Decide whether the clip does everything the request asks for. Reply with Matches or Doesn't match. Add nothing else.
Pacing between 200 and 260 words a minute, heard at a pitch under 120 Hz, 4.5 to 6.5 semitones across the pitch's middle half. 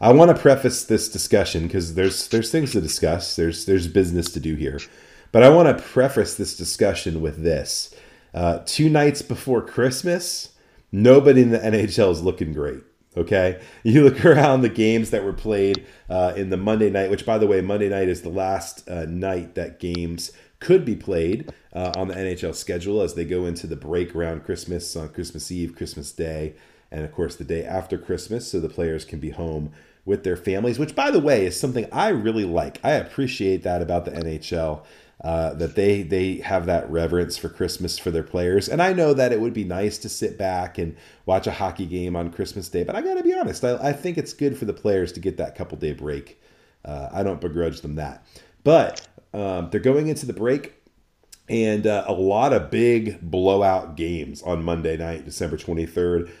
Matches